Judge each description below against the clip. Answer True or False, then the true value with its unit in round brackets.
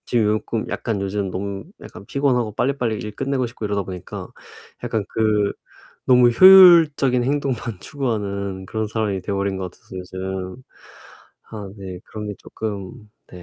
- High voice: False (105 Hz)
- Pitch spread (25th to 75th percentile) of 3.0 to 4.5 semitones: True (4.0 semitones)